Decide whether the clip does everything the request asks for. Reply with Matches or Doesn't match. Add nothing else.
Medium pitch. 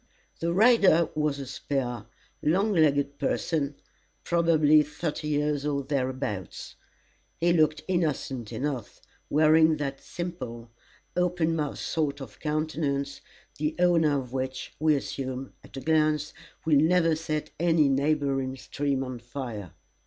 Matches